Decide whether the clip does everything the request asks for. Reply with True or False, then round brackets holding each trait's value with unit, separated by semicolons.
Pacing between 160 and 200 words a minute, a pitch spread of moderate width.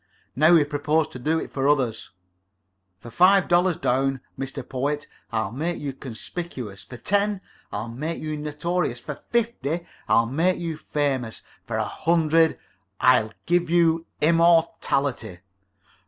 False (140 wpm; 4.5 semitones)